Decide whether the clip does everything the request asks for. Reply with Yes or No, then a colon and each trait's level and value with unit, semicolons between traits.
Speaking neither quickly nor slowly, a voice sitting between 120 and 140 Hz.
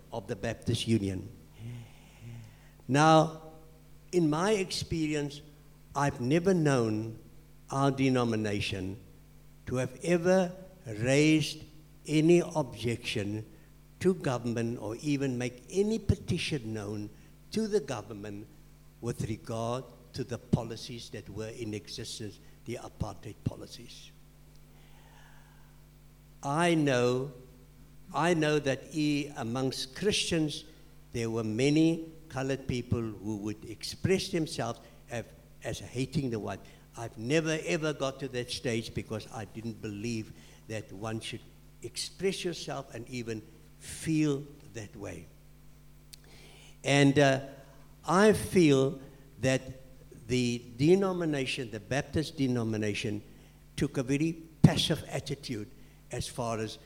No: slow, 110 wpm; low, 135 Hz